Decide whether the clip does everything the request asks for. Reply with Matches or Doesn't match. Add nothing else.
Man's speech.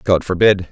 Matches